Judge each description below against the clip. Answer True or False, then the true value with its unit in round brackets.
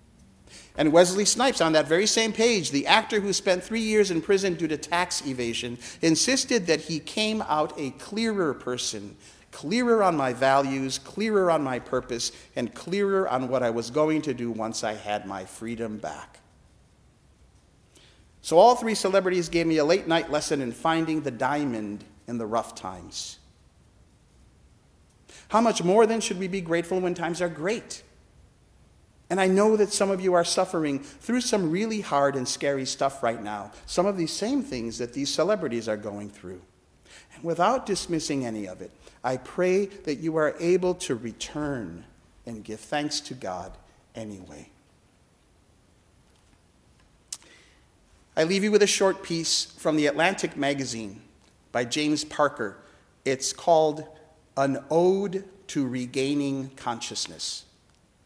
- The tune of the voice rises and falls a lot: True (7.7 semitones)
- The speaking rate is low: False (155 wpm)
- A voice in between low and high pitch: True (150 Hz)